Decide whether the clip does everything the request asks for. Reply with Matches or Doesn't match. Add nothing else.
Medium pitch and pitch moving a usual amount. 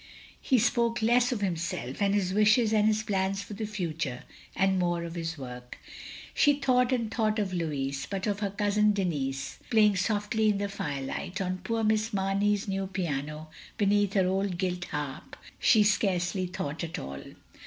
Doesn't match